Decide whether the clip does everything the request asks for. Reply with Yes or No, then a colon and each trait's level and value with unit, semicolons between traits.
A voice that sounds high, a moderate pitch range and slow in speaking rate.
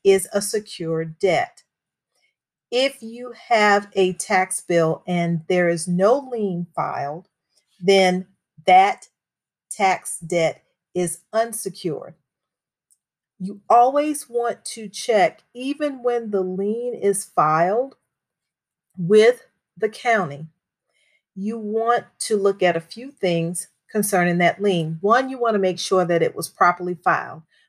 Yes: high, 195 Hz; average, 4.4 semitones; slow, 125 wpm